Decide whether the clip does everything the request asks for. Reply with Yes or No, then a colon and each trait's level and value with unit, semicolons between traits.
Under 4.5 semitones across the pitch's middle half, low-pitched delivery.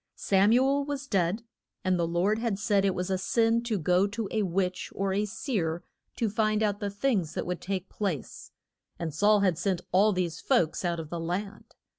No: average, 3.2 semitones; high, 195 Hz